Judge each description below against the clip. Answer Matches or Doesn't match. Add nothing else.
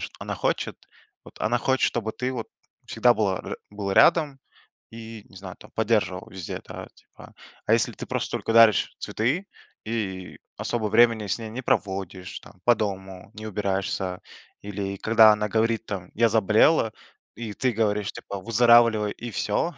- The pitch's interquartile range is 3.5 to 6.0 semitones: Doesn't match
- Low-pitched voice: Matches